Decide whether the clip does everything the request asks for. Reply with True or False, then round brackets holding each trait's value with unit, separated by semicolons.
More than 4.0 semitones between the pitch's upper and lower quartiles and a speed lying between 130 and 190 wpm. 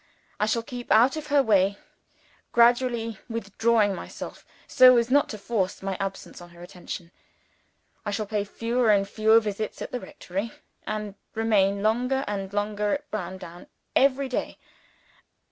False (3.2 semitones; 150 wpm)